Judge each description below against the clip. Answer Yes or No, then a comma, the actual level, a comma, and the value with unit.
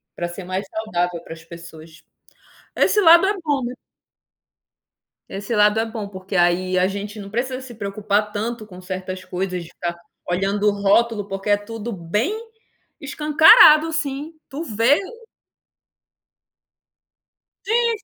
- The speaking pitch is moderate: No, high, 205 Hz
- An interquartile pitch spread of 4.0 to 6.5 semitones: Yes, wide, 5.6 semitones